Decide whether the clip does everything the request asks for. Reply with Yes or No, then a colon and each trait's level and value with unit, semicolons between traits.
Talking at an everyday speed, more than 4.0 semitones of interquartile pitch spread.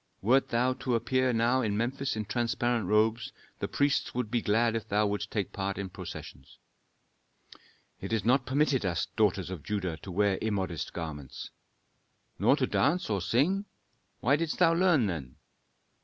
Yes: average, 165 wpm; average, 4.6 semitones